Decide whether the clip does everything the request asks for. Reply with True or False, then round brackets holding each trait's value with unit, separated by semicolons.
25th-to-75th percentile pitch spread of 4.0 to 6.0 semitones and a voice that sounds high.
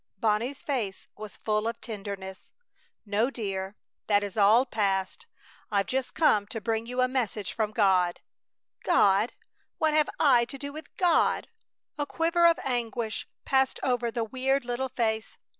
True (4.4 semitones; 230 Hz)